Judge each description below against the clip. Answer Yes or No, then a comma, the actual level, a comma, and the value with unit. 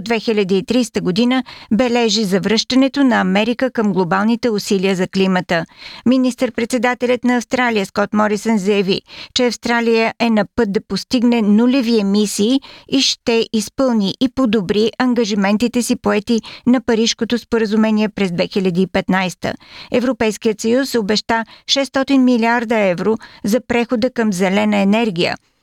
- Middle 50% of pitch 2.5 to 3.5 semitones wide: Yes, average, 3.1 semitones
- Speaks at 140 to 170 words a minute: No, slow, 115 wpm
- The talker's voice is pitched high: Yes, high, 230 Hz